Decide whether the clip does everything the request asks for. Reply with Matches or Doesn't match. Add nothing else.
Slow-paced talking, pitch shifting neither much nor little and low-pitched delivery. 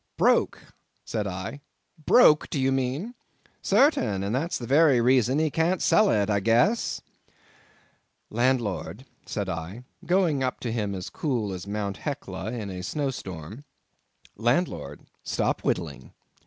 Doesn't match